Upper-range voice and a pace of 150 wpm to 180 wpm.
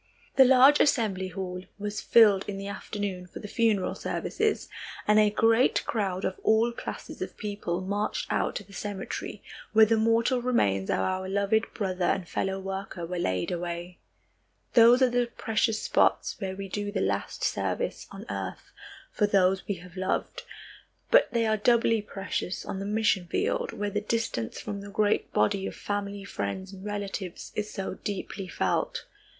Yes: high, 205 Hz; average, 170 wpm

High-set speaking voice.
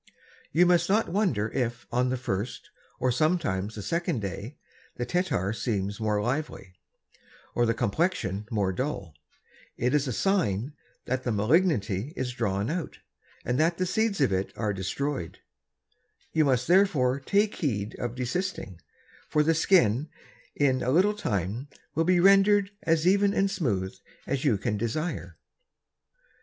No: low, 130 Hz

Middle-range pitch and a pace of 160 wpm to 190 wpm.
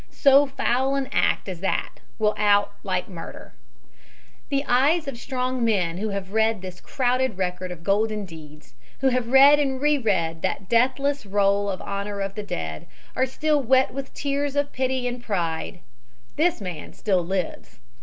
No: high, 225 Hz; average, 175 wpm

